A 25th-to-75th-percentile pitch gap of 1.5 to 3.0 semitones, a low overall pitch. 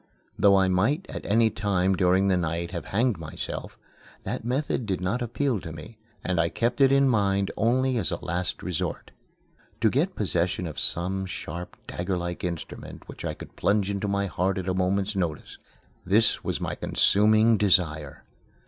No: average, 3.7 semitones; very low, 95 Hz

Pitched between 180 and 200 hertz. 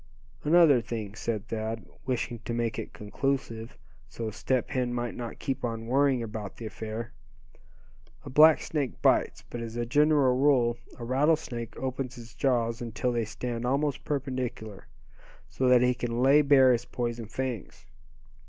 No: low, 120 Hz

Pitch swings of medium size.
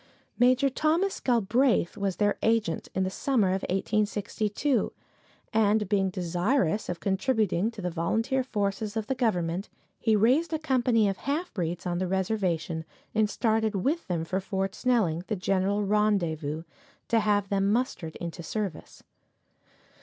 Yes: average, 3.8 semitones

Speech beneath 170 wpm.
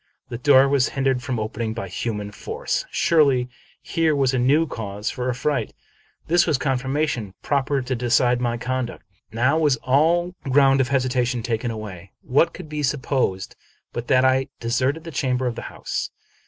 No: average, 175 wpm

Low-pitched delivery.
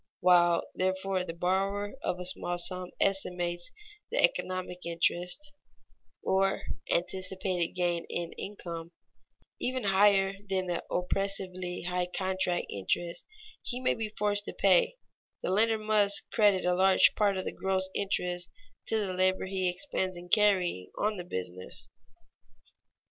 No: medium, 185 Hz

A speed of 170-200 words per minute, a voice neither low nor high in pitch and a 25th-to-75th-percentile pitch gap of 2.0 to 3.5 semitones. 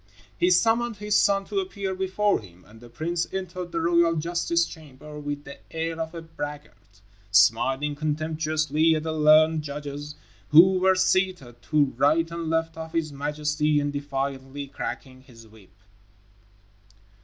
No: average, 150 wpm; medium, 155 Hz; average, 3.2 semitones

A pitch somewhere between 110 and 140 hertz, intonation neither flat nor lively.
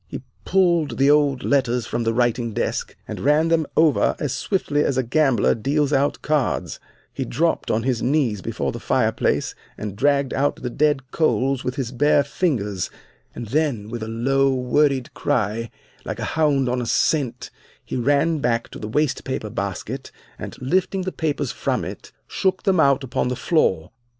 Yes: low, 135 Hz; average, 3.9 semitones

